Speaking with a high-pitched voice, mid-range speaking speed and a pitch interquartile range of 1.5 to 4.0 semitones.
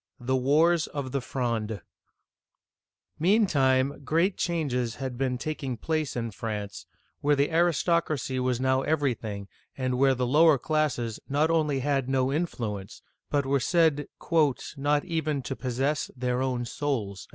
No: low, 135 Hz; average, 145 wpm; average, 3.5 semitones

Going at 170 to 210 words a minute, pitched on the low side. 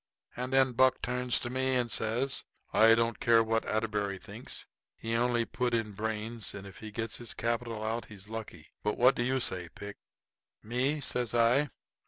Yes: average, 185 wpm; low, 115 Hz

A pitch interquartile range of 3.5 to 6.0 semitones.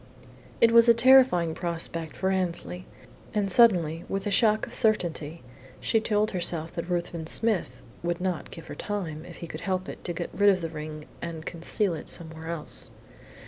Yes: average, 3.9 semitones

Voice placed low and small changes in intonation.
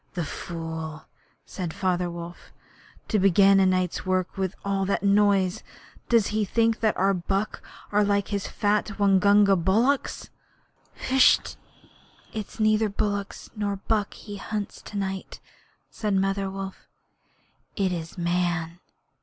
No: high, 195 Hz; narrow, 2.1 semitones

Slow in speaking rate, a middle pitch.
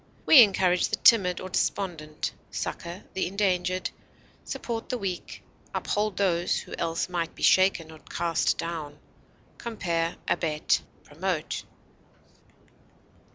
Yes: slow, 110 wpm; medium, 180 Hz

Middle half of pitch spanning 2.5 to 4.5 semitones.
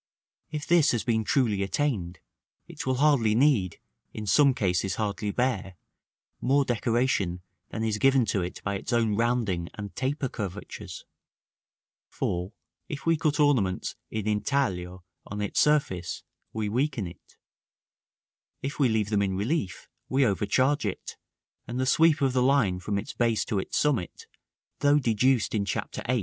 No: average, 5.2 semitones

